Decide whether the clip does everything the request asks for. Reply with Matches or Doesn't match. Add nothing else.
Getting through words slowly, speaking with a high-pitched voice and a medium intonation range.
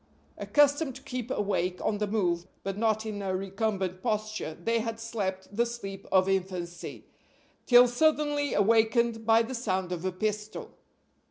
Doesn't match